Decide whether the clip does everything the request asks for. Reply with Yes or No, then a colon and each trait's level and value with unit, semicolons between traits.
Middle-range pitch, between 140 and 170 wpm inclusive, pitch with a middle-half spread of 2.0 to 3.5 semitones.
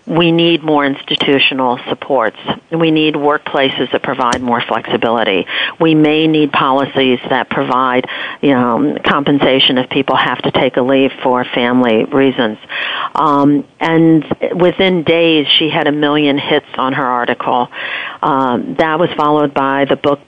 Yes: medium, 145 Hz; average, 150 wpm; average, 2.9 semitones